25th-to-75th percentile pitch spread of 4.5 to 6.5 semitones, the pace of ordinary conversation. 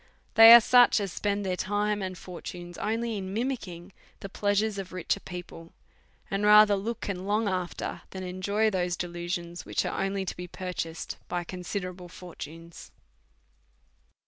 No: narrow, 2.6 semitones; average, 155 wpm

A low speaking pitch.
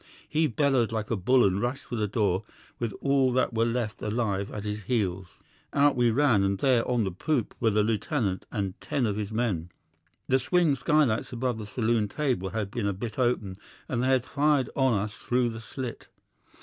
Yes: low, 115 Hz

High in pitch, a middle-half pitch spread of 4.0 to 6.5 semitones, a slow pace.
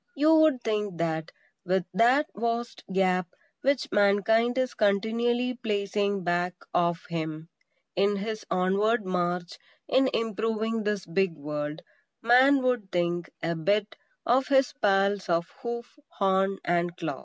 Yes: high, 200 Hz; average, 5.0 semitones; slow, 130 wpm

